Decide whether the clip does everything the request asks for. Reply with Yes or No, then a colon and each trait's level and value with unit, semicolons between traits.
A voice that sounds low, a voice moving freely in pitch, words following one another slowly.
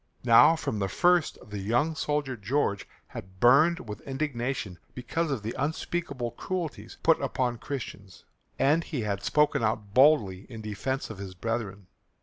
No: low, 120 Hz; wide, 6.1 semitones; average, 150 wpm